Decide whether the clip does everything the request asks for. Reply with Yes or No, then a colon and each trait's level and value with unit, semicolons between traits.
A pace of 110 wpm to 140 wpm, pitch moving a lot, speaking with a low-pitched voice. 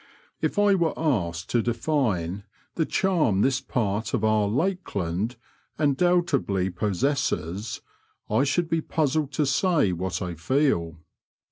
Yes: slow, 135 wpm; wide, 8.5 semitones; low, 120 Hz